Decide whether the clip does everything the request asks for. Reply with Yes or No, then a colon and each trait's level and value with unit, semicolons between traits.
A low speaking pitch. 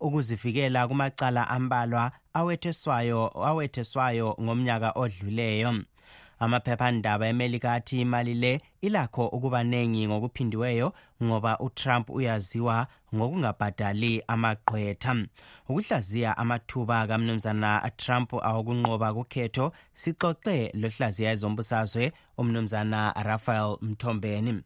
Yes: low, 120 Hz